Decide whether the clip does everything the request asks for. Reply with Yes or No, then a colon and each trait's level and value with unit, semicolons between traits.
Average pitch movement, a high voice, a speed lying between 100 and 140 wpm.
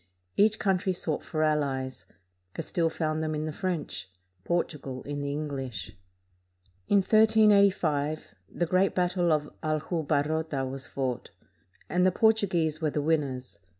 No: average, 4.0 semitones; medium, 155 Hz; slow, 135 wpm